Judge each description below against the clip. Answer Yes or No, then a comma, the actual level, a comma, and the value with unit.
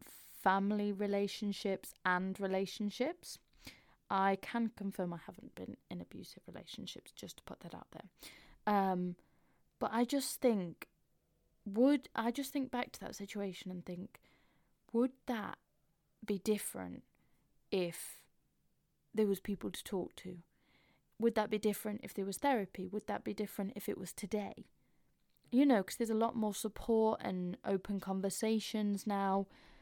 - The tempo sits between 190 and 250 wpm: No, average, 145 wpm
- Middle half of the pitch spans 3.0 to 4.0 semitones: No, narrow, 2.4 semitones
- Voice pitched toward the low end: No, high, 205 Hz